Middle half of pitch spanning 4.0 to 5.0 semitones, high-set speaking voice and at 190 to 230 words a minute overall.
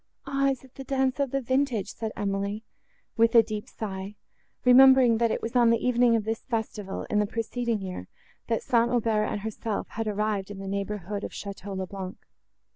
No: average, 3.2 semitones; high, 225 Hz; average, 200 wpm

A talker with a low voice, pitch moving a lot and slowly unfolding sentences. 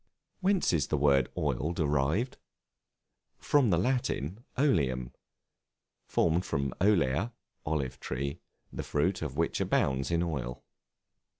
Yes: very low, 80 Hz; wide, 5.9 semitones; slow, 115 wpm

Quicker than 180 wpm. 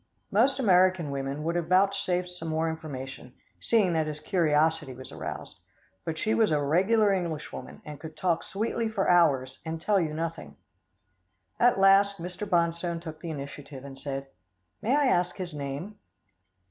No: average, 160 wpm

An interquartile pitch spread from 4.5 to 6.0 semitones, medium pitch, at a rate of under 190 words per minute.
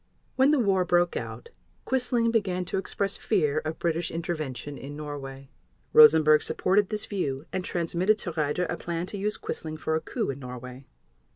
Yes: average, 4.8 semitones; medium, 170 Hz; average, 175 wpm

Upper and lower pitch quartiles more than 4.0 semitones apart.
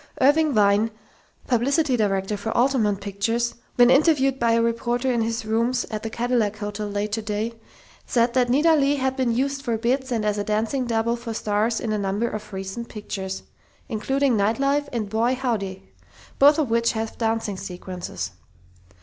No: average, 3.5 semitones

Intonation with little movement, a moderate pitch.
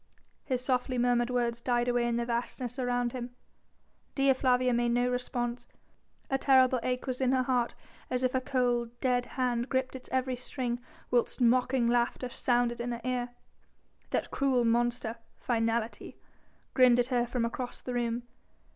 No: narrow, 1.1 semitones; high, 245 Hz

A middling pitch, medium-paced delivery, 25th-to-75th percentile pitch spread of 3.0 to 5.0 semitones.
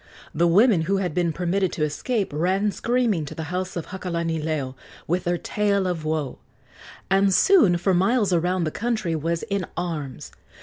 Yes: medium, 180 Hz; average, 170 wpm; average, 3.3 semitones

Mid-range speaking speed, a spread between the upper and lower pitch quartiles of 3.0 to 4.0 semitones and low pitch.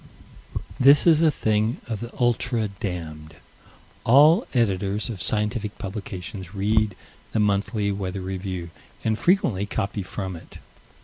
No: slow, 125 wpm; average, 3.3 semitones; low, 105 Hz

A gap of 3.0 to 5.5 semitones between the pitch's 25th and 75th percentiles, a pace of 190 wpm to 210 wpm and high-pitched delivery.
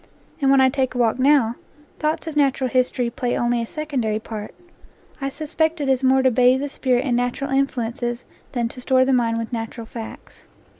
No: narrow, 2.4 semitones; average, 200 wpm; very high, 255 Hz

